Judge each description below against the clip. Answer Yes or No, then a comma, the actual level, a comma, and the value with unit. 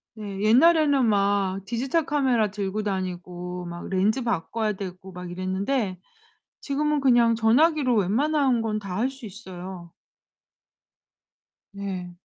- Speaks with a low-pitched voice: No, high, 210 Hz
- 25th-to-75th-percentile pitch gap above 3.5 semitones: Yes, average, 5.2 semitones